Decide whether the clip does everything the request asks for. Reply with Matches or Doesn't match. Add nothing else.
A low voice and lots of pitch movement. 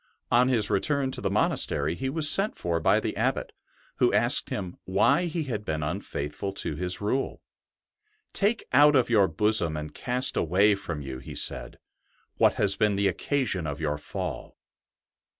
Matches